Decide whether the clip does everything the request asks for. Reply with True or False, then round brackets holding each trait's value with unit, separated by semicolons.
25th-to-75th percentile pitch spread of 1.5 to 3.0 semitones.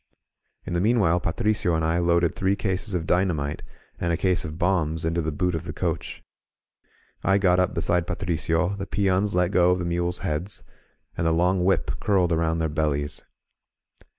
True (2.4 semitones)